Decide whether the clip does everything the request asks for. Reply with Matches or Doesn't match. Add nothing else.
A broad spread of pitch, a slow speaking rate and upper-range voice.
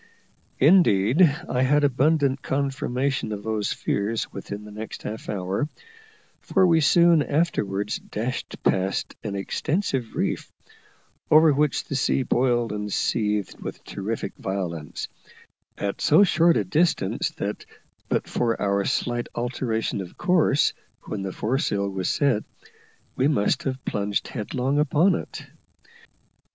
Doesn't match